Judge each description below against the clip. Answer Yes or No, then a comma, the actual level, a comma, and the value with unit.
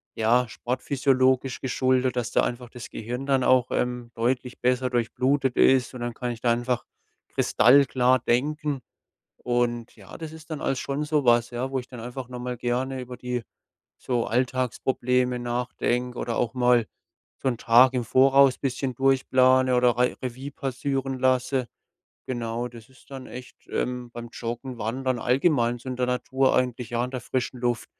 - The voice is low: Yes, low, 125 Hz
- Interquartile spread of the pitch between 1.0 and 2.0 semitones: Yes, narrow, 1.3 semitones